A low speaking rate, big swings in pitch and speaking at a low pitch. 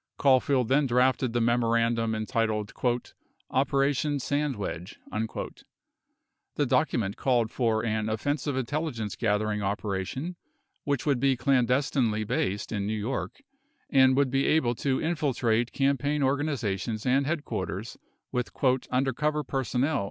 No: slow, 120 wpm; average, 4.0 semitones; low, 125 Hz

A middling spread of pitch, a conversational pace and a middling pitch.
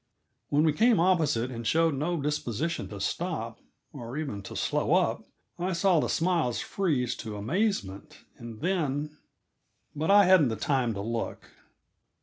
No: wide, 6.6 semitones; average, 150 wpm; medium, 150 Hz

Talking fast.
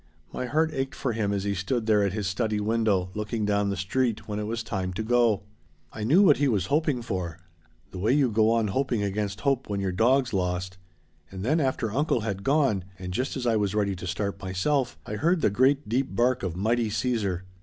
Yes: fast, 225 wpm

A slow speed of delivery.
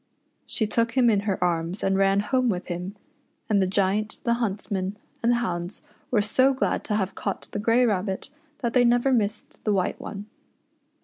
No: average, 190 wpm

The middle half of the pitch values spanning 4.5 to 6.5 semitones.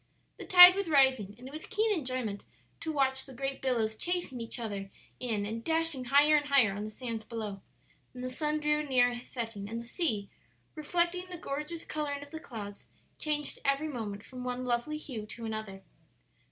Yes: average, 5.1 semitones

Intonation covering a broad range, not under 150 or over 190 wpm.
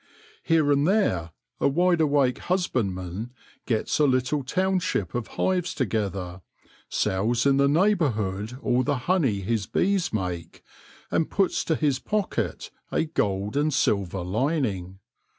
No: wide, 8.3 semitones; slow, 135 wpm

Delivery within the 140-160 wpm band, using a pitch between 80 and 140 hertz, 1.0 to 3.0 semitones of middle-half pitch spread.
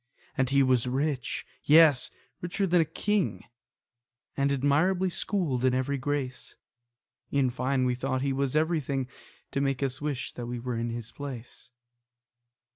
Yes: average, 155 wpm; low, 135 Hz; average, 2.7 semitones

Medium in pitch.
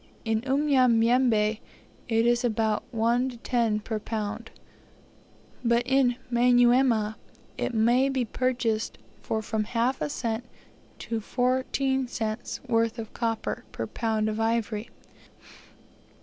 No: high, 235 Hz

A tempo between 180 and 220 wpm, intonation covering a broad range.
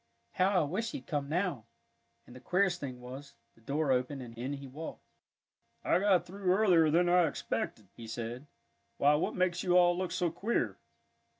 Yes: average, 185 wpm; wide, 6.0 semitones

